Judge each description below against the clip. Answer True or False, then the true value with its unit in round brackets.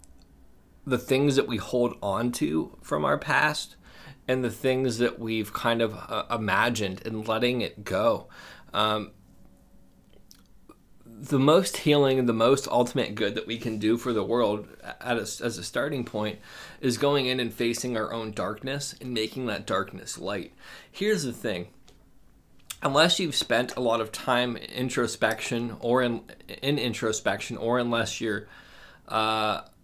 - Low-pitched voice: True (115 Hz)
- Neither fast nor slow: True (155 wpm)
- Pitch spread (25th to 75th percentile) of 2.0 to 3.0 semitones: True (2.6 semitones)